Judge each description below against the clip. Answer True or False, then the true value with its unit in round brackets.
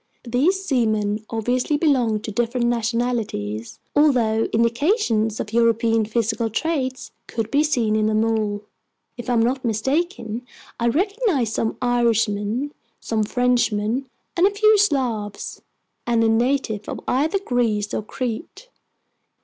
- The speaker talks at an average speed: False (125 wpm)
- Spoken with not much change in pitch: False (3.4 semitones)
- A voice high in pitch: True (235 Hz)